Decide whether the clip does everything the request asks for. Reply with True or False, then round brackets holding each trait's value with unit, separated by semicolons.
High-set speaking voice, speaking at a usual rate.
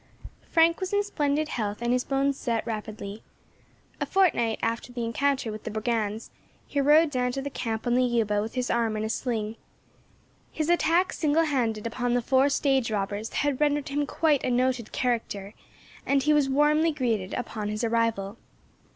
True (245 Hz; 180 wpm)